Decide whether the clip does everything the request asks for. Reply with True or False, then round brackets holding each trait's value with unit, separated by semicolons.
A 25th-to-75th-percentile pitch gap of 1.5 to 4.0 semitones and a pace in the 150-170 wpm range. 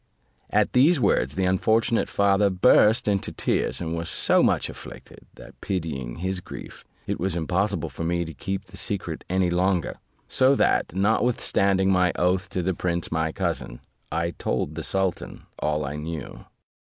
True (2.9 semitones; 165 wpm)